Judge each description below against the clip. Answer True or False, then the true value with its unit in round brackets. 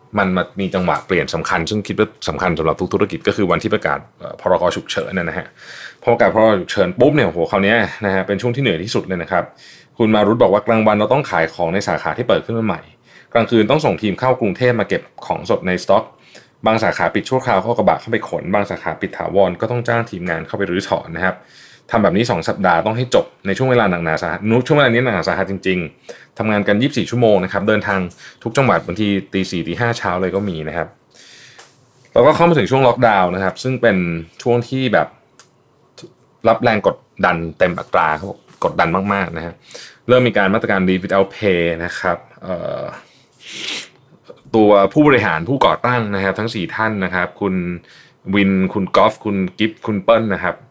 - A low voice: True (100 Hz)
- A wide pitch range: False (3.8 semitones)